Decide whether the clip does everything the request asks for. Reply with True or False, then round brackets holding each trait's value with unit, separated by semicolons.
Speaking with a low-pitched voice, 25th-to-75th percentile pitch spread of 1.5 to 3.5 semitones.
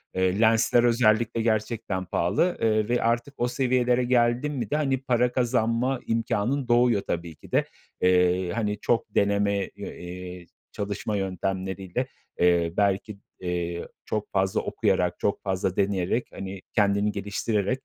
False (105 Hz; 4.0 semitones)